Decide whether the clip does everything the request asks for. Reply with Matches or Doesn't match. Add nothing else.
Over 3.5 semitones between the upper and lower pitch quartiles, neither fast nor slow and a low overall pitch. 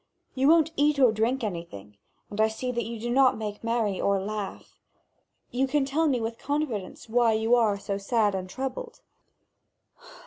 Doesn't match